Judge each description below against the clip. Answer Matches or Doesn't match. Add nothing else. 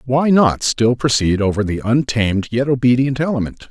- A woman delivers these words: Doesn't match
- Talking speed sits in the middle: Matches